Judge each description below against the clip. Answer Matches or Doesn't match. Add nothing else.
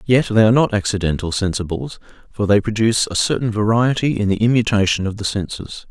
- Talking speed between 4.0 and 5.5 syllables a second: Doesn't match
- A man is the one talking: Matches